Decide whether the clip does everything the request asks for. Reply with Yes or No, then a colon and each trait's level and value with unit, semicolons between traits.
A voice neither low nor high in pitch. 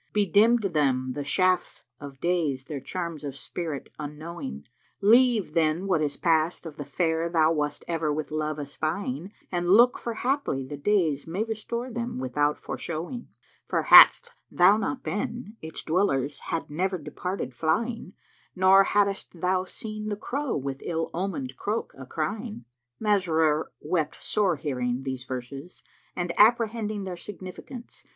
Yes: medium, 170 Hz